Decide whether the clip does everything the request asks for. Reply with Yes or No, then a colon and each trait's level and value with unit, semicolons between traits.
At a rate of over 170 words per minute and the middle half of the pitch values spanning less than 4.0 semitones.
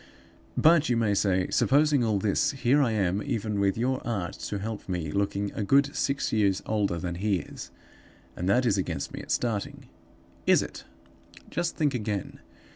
No: average, 180 wpm; average, 4.4 semitones